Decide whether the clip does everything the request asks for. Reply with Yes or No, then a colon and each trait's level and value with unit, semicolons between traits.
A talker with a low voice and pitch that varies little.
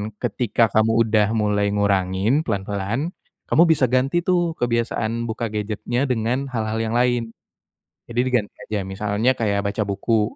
No: low, 115 Hz; average, 3.0 semitones